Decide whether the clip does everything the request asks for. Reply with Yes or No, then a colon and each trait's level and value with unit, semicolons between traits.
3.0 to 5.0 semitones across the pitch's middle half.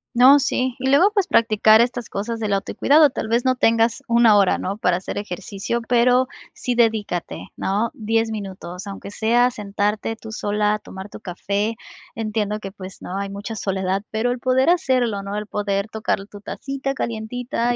Yes: average, 3.3 semitones